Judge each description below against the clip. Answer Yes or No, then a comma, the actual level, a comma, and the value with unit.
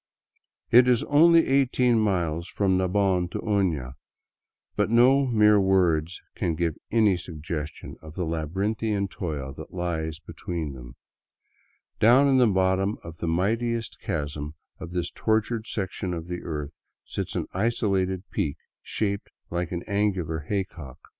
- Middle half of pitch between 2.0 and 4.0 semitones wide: No, average, 4.8 semitones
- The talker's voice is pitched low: Yes, very low, 95 Hz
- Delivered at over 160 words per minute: No, average, 140 wpm